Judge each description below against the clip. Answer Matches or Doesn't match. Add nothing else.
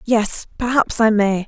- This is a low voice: Doesn't match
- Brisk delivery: Doesn't match